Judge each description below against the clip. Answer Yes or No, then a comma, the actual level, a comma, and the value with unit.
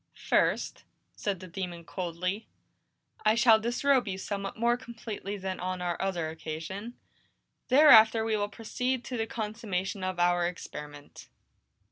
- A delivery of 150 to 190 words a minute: No, slow, 135 wpm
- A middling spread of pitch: Yes, average, 4.0 semitones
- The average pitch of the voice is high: Yes, high, 200 Hz